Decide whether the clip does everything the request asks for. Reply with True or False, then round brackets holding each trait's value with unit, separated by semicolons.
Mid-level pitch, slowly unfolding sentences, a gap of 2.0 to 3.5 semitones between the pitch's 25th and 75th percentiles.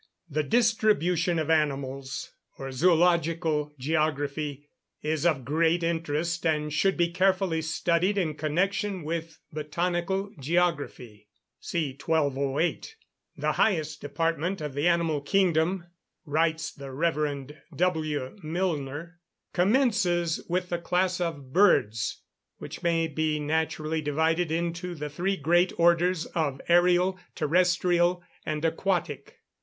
True (165 Hz; 115 wpm; 2.9 semitones)